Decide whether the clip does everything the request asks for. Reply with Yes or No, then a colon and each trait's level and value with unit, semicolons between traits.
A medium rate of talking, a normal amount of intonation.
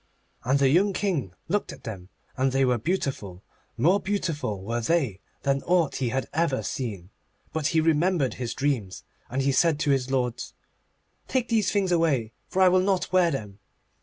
No: average, 185 wpm; wide, 6.3 semitones